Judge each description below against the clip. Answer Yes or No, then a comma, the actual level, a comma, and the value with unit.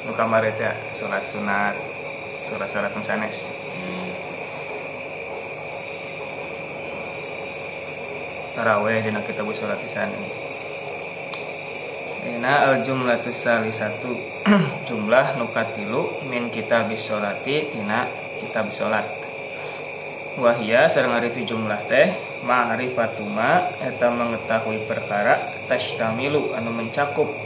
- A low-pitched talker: Yes, low, 115 Hz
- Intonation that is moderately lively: Yes, average, 3.0 semitones